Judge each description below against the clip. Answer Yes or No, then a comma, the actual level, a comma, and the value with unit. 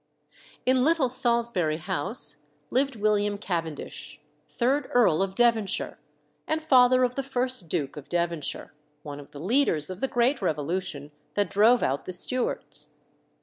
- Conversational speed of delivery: Yes, average, 145 wpm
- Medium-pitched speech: No, high, 205 Hz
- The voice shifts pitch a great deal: Yes, wide, 7.9 semitones